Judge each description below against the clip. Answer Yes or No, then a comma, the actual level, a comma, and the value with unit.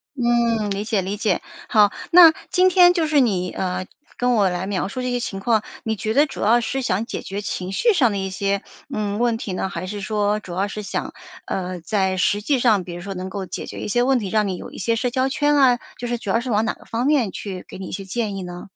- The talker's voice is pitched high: Yes, high, 210 Hz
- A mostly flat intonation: No, average, 4.0 semitones